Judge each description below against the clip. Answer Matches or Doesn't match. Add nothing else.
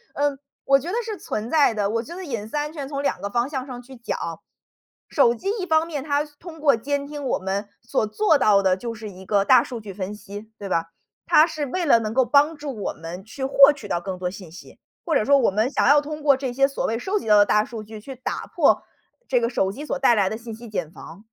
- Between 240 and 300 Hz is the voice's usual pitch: Matches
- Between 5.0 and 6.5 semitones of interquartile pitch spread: Matches